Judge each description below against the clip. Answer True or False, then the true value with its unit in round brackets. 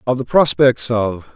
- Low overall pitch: True (125 Hz)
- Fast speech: False (175 wpm)